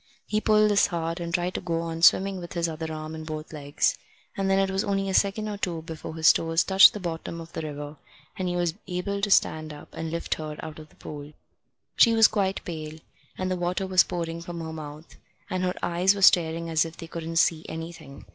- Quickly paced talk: Yes, fast, 235 wpm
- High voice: No, medium, 170 Hz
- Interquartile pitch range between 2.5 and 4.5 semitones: Yes, average, 2.9 semitones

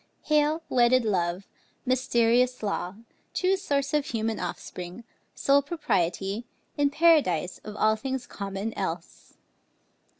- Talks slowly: Yes, slow, 110 wpm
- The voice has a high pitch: Yes, high, 235 Hz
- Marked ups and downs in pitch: Yes, wide, 6.4 semitones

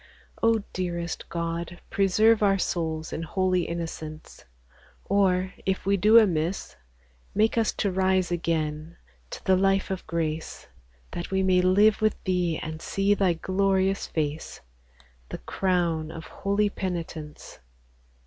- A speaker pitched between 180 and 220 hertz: Yes, medium, 185 Hz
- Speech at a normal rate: No, slow, 130 wpm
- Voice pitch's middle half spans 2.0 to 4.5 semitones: Yes, average, 2.9 semitones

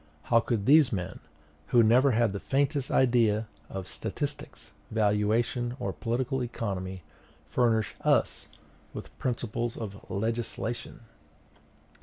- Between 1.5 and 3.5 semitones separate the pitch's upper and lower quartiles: Yes, average, 2.8 semitones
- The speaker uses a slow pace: Yes, slow, 110 wpm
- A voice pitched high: No, low, 115 Hz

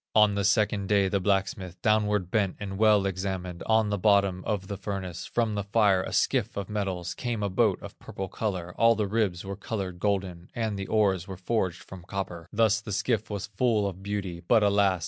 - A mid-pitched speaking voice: No, low, 100 Hz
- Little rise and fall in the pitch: Yes, narrow, 2.1 semitones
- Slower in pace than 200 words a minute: No, fast, 205 wpm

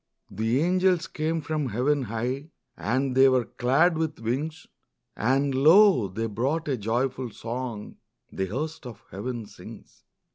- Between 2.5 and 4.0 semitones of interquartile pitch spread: No, average, 4.8 semitones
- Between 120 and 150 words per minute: Yes, average, 140 wpm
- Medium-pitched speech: No, low, 130 Hz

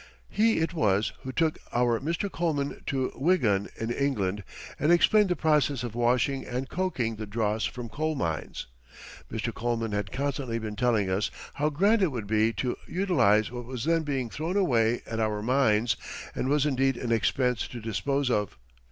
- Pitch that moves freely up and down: No, average, 4.9 semitones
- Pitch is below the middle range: Yes, low, 125 Hz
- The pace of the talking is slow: No, average, 180 wpm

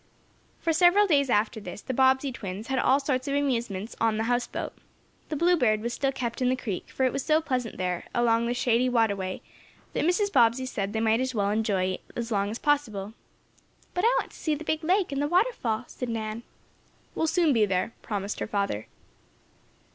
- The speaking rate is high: Yes, fast, 210 wpm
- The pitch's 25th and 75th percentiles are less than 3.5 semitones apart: No, average, 4.7 semitones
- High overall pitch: Yes, high, 245 Hz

